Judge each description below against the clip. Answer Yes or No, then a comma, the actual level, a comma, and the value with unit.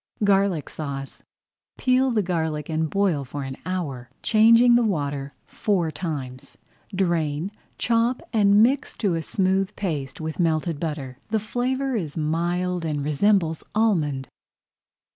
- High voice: No, medium, 170 Hz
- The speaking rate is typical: No, slow, 130 wpm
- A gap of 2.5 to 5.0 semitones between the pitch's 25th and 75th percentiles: No, wide, 5.6 semitones